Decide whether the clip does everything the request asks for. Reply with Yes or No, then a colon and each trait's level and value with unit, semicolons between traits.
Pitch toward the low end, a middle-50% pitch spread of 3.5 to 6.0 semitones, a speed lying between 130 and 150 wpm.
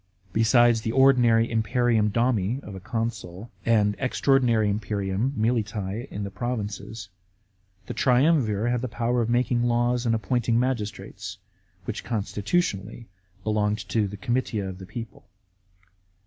No: low, 115 Hz; average, 2.8 semitones; average, 145 wpm